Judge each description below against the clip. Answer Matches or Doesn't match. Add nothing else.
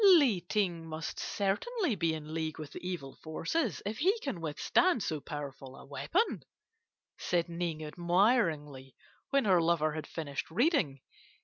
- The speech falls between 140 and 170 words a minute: Matches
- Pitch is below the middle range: Doesn't match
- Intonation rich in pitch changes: Matches